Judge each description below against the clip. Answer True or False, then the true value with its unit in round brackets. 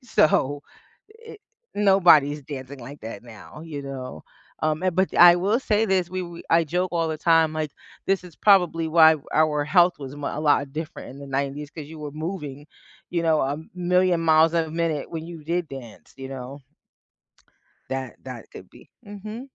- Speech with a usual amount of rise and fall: True (3.8 semitones)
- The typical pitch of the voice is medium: True (160 Hz)